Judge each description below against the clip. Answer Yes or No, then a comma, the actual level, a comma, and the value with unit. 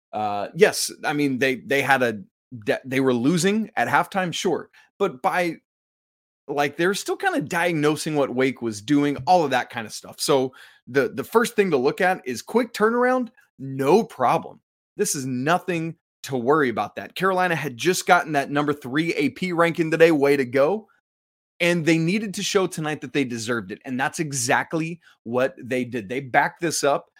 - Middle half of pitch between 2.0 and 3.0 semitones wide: No, average, 5.3 semitones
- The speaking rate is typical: Yes, average, 190 wpm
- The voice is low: No, medium, 155 Hz